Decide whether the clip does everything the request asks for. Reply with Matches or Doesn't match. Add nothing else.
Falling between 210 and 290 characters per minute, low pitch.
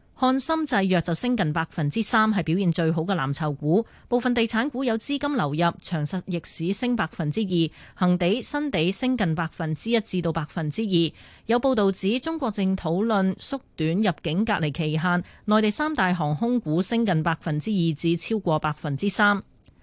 Doesn't match